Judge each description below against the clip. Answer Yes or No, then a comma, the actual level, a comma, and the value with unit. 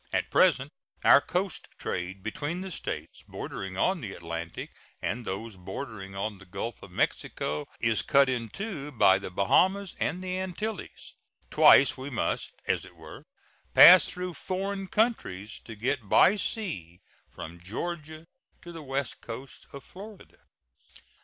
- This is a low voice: Yes, low, 130 Hz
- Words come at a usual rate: Yes, average, 145 wpm